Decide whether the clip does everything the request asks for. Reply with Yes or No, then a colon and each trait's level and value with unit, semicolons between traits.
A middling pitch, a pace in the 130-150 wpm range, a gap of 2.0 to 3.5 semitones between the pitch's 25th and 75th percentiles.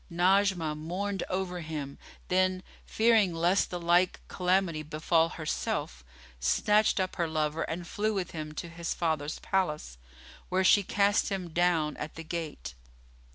Yes: medium, 175 Hz; average, 145 wpm; average, 3.2 semitones